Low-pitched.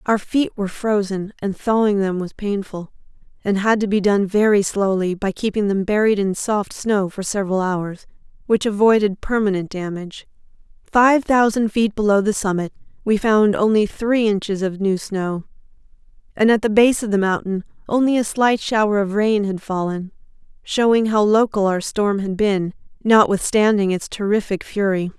No: high, 205 Hz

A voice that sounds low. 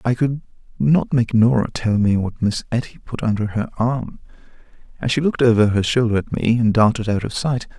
Yes: low, 115 Hz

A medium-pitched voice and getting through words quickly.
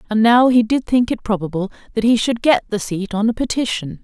No: high, 220 Hz; fast, 240 wpm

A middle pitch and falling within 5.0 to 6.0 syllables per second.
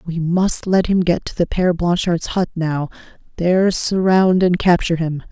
No: medium, 175 Hz; 4.8 syllables/s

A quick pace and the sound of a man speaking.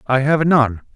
No: average, 190 wpm; male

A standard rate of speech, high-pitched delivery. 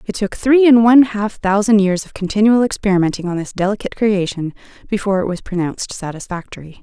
Yes: average, 175 wpm; high, 200 Hz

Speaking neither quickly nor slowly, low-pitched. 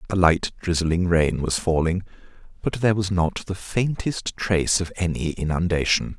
Yes: average, 155 wpm; very low, 90 Hz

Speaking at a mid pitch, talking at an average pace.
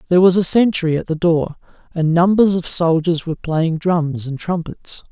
Yes: medium, 170 Hz; average, 190 wpm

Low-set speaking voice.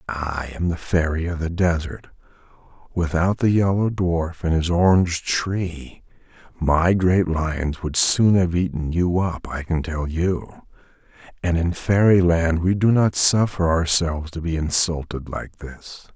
Yes: very low, 85 Hz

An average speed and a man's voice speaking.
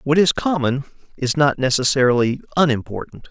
No: slow, 125 wpm; male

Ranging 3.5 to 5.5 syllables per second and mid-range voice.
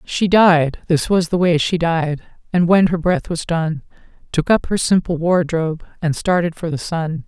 Yes: 4.6 syllables/s; medium, 170 Hz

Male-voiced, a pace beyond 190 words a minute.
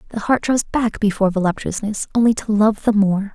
No: female; average, 200 wpm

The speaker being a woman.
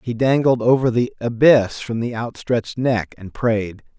No: male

